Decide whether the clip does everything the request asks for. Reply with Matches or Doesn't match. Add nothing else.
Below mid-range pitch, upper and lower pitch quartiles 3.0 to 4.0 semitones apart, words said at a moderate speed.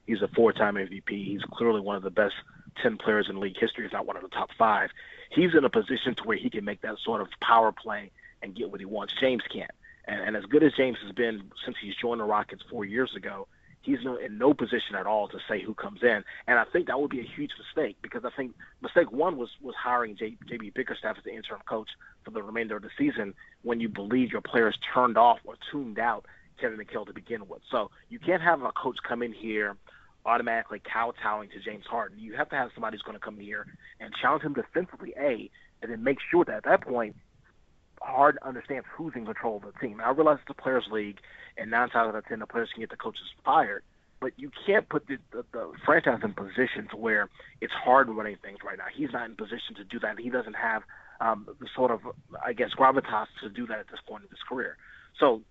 Doesn't match